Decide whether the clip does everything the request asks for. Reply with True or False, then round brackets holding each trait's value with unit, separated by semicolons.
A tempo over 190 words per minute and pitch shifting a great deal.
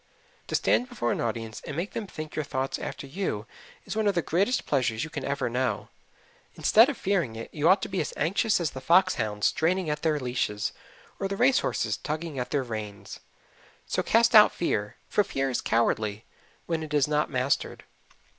True (200 wpm; 7.6 semitones)